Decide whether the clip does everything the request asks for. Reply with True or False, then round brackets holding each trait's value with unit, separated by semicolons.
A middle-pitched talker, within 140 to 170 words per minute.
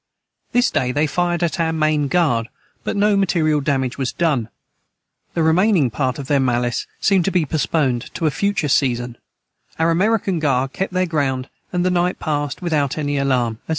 False (155 Hz; 185 wpm)